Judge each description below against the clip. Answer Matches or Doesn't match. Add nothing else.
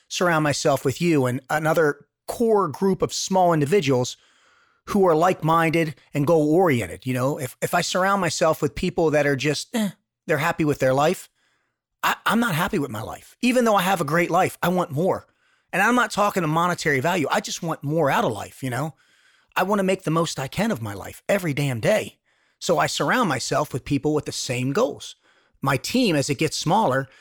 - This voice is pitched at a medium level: Matches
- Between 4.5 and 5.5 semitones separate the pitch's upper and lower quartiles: Matches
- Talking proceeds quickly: Matches